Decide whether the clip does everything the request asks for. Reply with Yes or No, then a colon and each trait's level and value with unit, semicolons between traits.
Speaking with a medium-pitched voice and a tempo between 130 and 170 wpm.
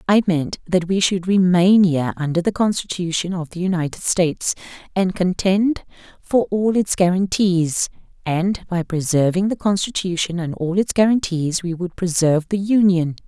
Yes: medium, 180 Hz; average, 155 wpm